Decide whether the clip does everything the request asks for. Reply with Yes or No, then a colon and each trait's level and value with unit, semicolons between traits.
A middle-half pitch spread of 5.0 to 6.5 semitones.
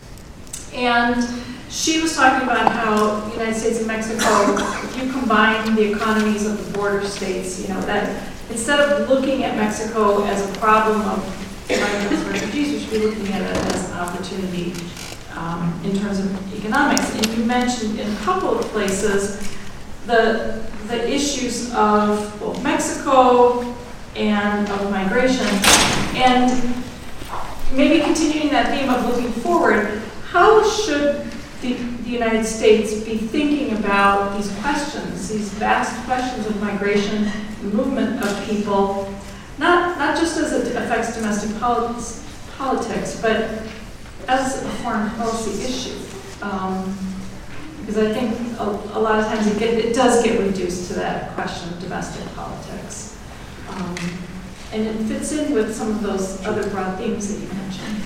No: average, 3.3 semitones